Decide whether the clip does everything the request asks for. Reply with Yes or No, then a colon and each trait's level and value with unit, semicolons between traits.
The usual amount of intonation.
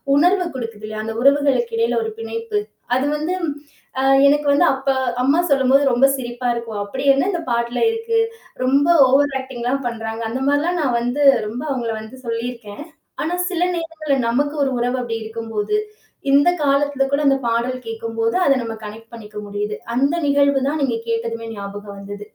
Yes: average, 4.0 semitones